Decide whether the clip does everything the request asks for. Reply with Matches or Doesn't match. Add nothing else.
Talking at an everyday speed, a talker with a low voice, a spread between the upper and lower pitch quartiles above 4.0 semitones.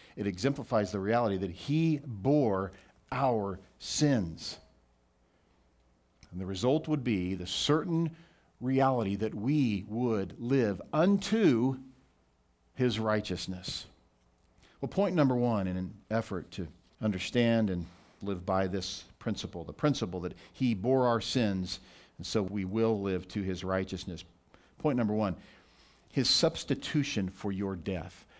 Doesn't match